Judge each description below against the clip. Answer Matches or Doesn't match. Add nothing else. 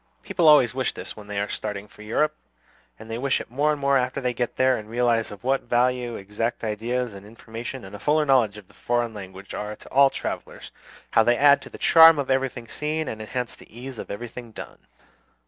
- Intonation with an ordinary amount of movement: Matches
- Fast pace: Matches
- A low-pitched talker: Matches